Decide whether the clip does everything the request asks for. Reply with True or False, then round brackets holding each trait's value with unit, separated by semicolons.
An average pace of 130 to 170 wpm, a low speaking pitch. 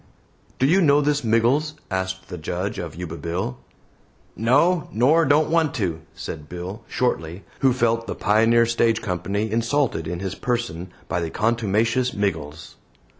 True (150 wpm; 110 Hz)